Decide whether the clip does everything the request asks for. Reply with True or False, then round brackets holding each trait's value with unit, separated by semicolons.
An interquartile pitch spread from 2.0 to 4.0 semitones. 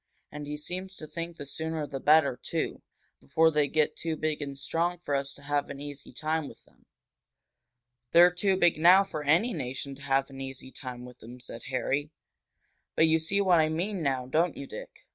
True (3.2 semitones)